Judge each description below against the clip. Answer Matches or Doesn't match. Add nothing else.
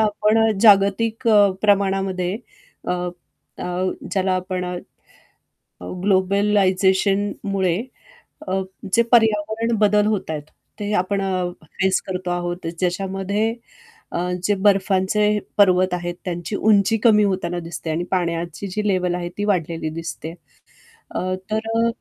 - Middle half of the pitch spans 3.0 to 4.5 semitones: Doesn't match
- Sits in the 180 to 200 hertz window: Matches